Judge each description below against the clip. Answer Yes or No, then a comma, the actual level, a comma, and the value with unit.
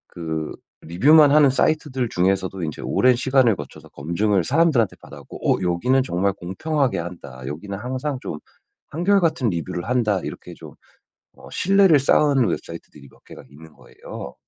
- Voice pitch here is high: No, low, 110 Hz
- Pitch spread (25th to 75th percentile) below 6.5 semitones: No, wide, 8.3 semitones